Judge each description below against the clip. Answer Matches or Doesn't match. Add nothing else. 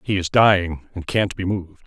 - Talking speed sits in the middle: Doesn't match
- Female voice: Doesn't match